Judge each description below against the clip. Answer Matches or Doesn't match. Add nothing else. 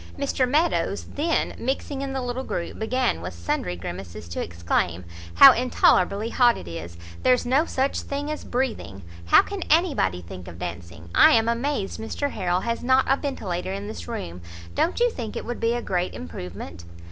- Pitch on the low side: Doesn't match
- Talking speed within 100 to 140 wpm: Doesn't match